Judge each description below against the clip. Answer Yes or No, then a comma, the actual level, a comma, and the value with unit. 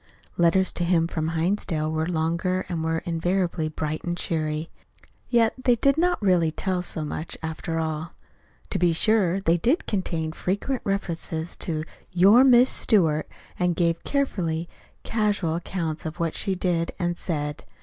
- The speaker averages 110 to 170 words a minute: Yes, average, 155 wpm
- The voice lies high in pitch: No, medium, 170 Hz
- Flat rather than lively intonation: No, average, 3.0 semitones